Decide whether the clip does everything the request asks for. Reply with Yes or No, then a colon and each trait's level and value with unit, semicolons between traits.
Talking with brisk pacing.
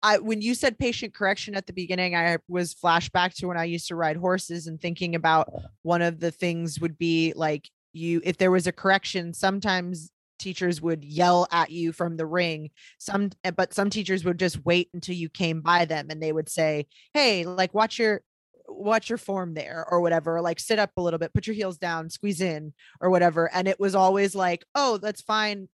Yes: fast, 215 wpm